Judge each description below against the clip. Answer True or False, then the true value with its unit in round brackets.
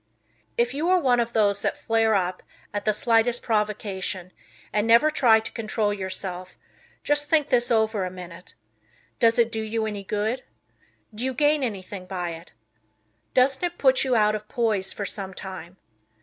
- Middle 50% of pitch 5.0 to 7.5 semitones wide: False (3.7 semitones)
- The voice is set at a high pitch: True (220 Hz)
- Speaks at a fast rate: False (175 wpm)